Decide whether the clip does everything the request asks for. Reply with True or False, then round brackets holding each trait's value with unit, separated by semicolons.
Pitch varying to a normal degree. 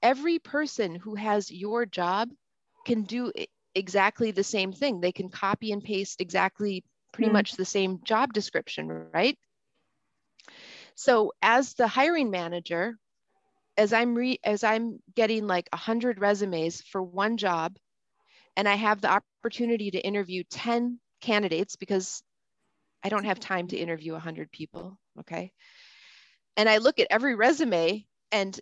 True (4.1 semitones)